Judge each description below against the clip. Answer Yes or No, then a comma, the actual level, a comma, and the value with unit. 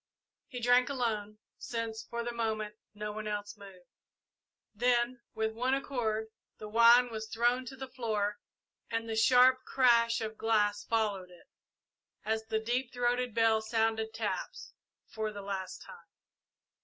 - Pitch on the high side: Yes, high, 225 Hz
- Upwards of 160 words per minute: No, average, 145 wpm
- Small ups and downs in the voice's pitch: Yes, narrow, 2.2 semitones